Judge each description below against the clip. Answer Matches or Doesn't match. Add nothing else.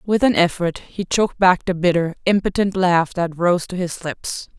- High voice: Doesn't match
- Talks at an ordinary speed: Matches